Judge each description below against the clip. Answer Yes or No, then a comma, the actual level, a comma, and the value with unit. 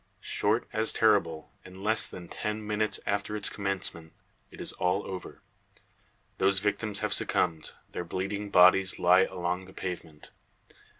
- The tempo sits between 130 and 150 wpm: Yes, average, 140 wpm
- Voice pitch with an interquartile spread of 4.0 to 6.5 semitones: No, narrow, 2.6 semitones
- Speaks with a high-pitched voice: No, very low, 95 Hz